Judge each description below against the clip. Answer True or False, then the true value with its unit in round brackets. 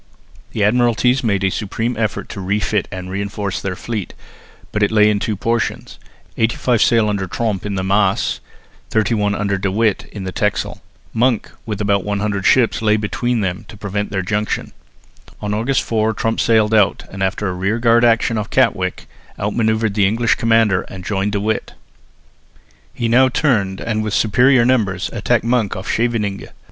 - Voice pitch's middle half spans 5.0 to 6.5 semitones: False (2.4 semitones)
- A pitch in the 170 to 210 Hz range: False (105 Hz)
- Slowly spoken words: False (175 wpm)